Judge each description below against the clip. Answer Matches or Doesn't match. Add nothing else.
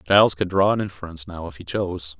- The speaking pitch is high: Doesn't match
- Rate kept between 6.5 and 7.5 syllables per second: Matches